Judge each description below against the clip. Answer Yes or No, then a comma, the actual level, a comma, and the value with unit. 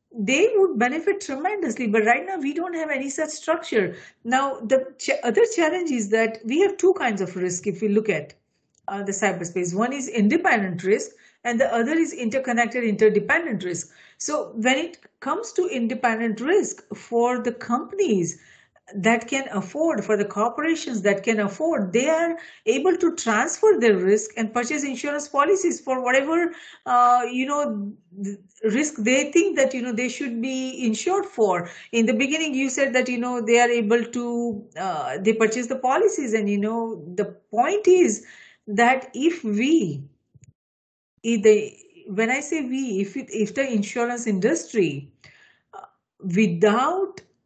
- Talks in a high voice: Yes, high, 245 Hz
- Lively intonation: Yes, wide, 6.4 semitones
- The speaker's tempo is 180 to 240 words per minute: No, average, 165 wpm